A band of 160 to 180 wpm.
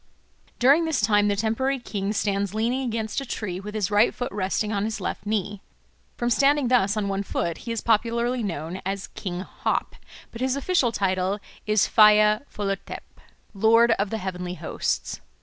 Yes: average, 175 wpm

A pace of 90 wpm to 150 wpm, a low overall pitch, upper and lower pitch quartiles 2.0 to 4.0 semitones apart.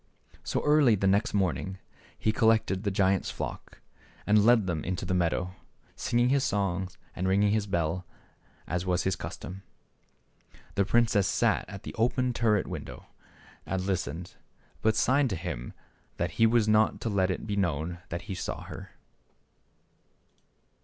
No: average, 160 wpm; very low, 95 Hz; average, 3.3 semitones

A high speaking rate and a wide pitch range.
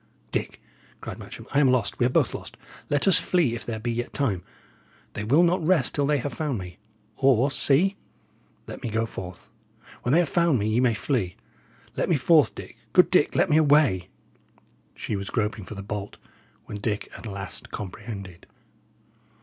No: average, 190 wpm; wide, 6.0 semitones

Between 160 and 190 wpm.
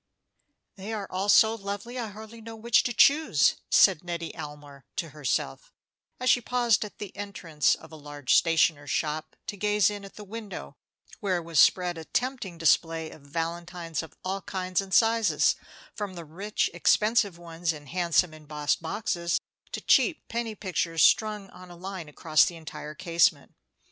Yes: average, 170 wpm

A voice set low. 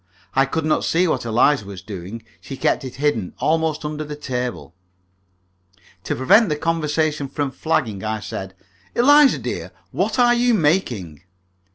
No: medium, 150 Hz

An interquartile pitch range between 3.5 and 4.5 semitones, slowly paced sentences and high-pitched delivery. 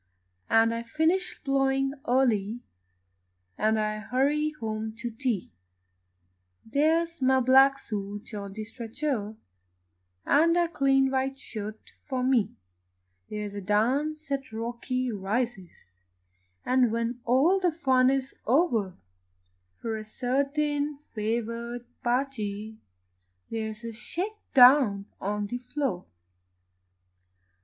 Yes: average, 3.9 semitones; slow, 110 wpm; high, 245 Hz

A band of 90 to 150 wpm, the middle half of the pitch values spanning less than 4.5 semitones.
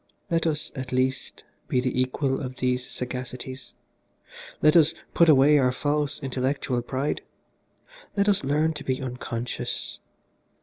Yes: slow, 135 wpm; average, 2.7 semitones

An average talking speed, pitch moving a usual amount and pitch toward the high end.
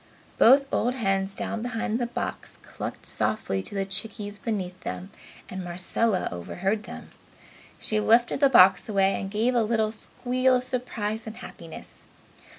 Yes: average, 155 wpm; average, 3.6 semitones; high, 215 Hz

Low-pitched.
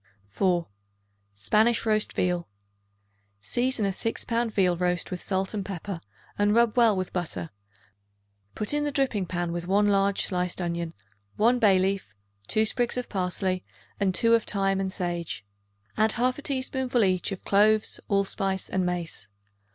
No: high, 195 Hz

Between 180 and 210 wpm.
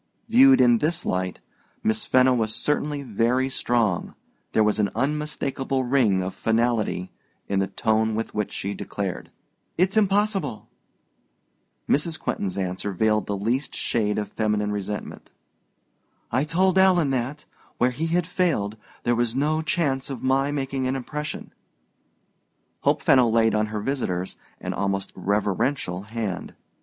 No: average, 140 wpm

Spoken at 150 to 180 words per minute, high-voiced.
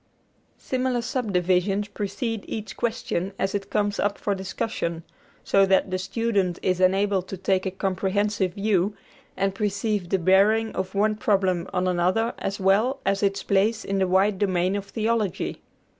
Yes: average, 160 wpm; high, 195 Hz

